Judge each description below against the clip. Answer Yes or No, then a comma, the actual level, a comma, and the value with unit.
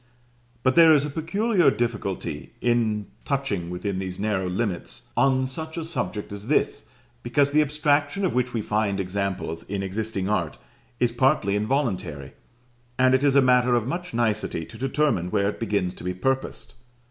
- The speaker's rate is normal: Yes, average, 170 wpm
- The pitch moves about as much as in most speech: No, wide, 5.8 semitones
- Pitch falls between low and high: No, low, 120 Hz